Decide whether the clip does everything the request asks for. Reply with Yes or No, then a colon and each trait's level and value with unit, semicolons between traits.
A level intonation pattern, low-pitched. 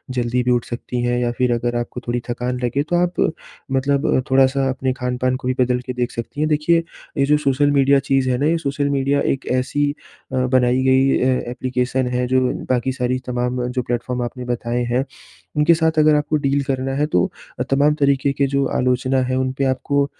Yes: narrow, 1.9 semitones; low, 130 Hz